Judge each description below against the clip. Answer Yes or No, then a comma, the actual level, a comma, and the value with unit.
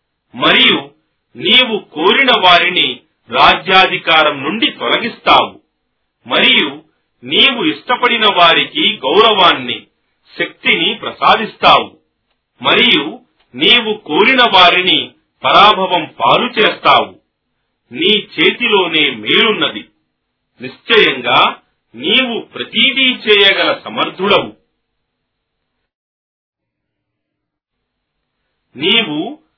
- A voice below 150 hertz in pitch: No, high, 200 Hz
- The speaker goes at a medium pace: No, slow, 60 wpm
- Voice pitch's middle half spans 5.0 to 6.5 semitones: Yes, wide, 5.4 semitones